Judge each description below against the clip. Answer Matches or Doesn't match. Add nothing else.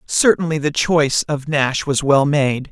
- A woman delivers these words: Doesn't match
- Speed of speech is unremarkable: Matches